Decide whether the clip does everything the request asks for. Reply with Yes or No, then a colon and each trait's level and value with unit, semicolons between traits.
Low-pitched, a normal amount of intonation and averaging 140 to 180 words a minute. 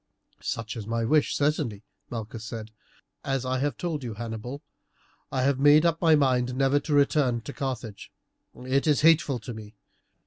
Yes: low, 130 Hz; average, 4.1 semitones; average, 170 wpm